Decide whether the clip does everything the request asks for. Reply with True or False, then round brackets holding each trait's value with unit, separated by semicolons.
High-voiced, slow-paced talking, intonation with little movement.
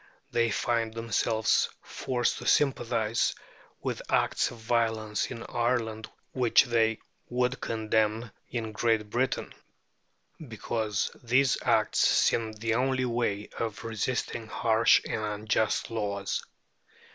False (115 Hz; 110 wpm; 1.5 semitones)